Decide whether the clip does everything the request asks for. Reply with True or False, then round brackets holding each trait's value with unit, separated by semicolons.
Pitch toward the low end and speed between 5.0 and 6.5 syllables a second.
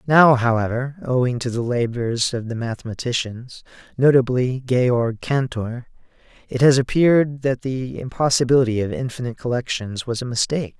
True (125 Hz; 5.1 syllables/s)